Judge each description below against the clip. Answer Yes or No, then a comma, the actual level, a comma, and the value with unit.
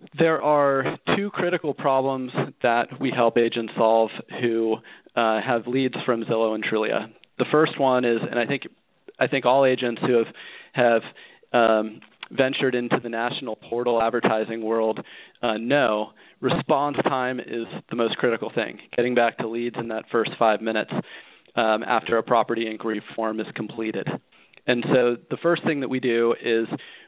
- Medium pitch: No, low, 120 Hz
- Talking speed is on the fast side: No, average, 165 wpm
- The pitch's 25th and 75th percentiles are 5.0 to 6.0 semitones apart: No, narrow, 2.6 semitones